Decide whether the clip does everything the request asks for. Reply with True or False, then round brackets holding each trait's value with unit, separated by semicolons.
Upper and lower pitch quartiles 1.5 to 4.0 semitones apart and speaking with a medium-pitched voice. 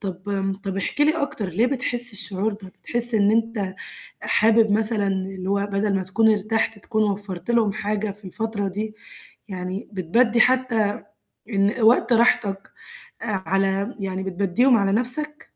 False (2.7 semitones; 205 Hz)